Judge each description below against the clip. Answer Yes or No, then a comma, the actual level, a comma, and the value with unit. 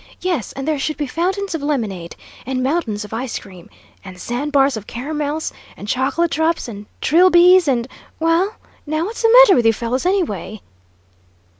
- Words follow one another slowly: No, average, 165 wpm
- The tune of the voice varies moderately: No, wide, 6.5 semitones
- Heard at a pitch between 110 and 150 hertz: No, very high, 285 Hz